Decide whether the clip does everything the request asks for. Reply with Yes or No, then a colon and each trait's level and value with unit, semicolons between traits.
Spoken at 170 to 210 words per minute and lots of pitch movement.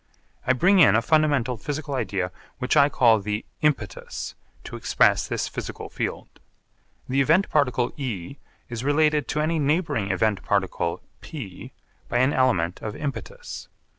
No: average, 145 wpm; wide, 6.1 semitones